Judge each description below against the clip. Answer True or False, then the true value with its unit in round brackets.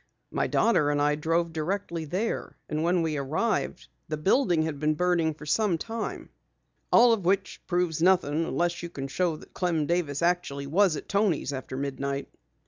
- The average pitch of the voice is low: False (165 Hz)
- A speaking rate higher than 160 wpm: True (175 wpm)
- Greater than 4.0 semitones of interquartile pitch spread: False (3.4 semitones)